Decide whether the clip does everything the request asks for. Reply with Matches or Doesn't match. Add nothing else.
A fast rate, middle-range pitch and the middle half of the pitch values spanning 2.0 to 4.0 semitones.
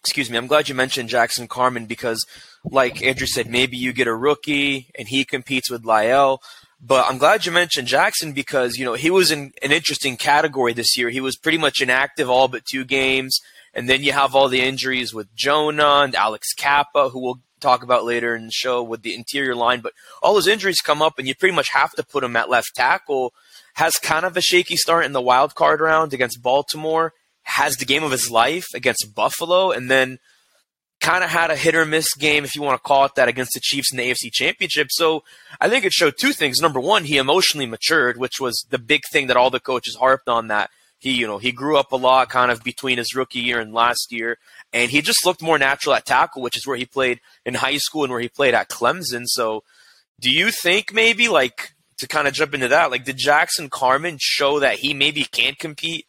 Doesn't match